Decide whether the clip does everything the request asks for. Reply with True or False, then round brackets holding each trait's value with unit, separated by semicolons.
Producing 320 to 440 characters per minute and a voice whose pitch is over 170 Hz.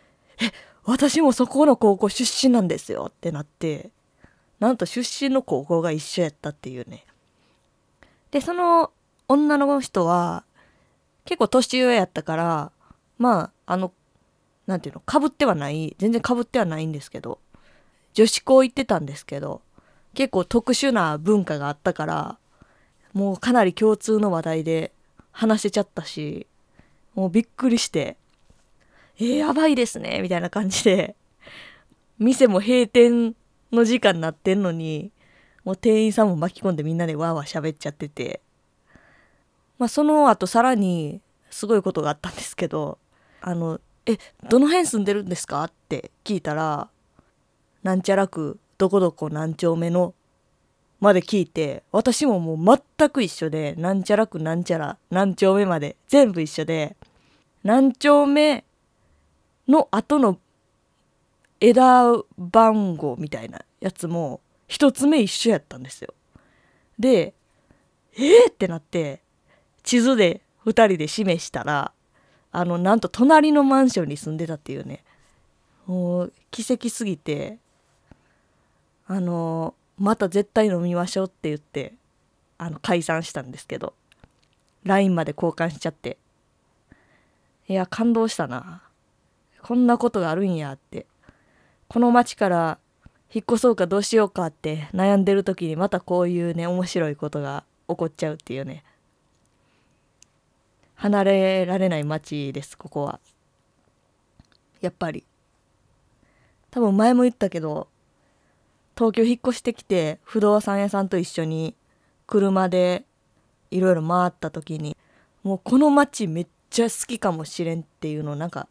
False (275 characters per minute; 190 Hz)